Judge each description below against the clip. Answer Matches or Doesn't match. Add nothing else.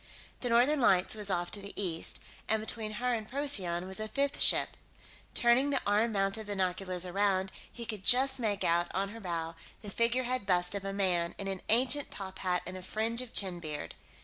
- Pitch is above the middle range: Matches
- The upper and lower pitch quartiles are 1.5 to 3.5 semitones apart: Doesn't match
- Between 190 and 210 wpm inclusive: Matches